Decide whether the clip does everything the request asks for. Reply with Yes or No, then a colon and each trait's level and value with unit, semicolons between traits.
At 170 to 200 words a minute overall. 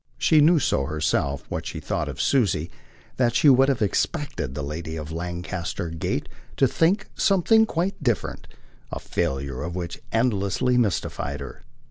No: average, 155 wpm